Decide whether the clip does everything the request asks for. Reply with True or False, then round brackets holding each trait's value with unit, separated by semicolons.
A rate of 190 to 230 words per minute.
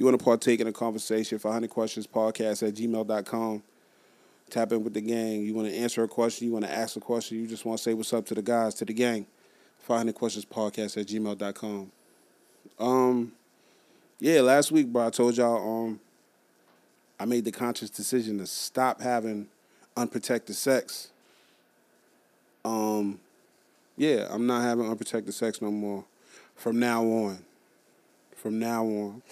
False (165 wpm)